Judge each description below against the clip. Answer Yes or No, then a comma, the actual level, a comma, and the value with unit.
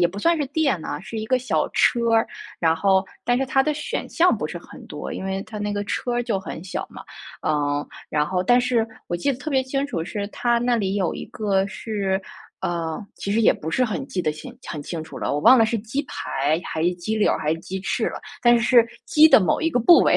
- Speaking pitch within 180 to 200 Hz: No, high, 210 Hz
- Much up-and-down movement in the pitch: Yes, wide, 5.7 semitones